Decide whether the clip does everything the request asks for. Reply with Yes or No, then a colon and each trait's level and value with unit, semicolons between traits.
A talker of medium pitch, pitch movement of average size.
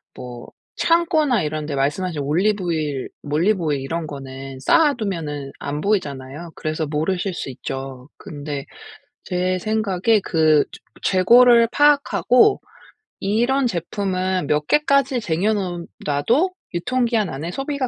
No: medium, 180 Hz; wide, 7.5 semitones